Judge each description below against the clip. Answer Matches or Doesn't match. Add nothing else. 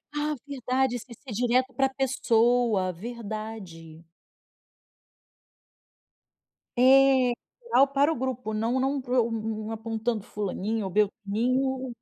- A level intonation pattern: Doesn't match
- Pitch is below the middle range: Doesn't match